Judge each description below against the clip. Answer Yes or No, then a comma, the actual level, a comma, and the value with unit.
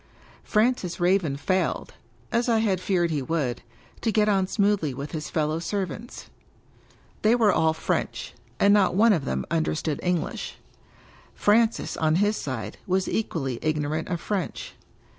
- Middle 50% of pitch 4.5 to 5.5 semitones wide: Yes, average, 5.0 semitones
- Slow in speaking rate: No, average, 155 wpm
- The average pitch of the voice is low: No, medium, 180 Hz